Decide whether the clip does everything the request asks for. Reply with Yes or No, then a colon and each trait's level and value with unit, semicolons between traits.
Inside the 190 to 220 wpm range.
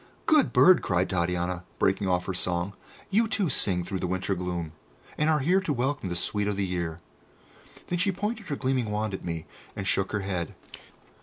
Yes: average, 200 wpm